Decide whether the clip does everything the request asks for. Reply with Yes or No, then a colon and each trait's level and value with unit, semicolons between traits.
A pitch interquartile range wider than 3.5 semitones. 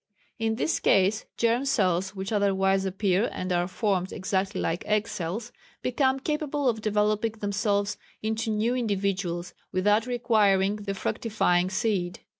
No: average, 2.8 semitones